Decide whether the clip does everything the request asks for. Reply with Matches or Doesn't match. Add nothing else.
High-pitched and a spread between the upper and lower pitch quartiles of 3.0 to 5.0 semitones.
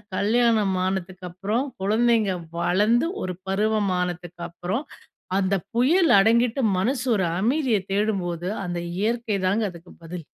Matches